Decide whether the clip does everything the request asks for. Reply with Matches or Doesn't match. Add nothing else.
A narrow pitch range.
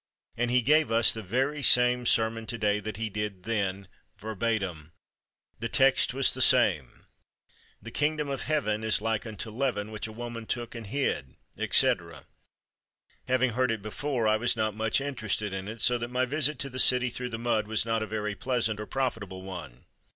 Doesn't match